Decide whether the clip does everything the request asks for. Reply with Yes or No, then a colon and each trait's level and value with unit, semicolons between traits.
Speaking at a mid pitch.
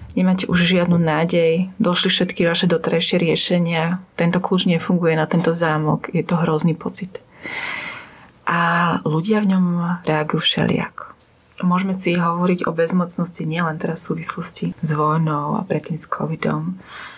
Yes: medium, 170 Hz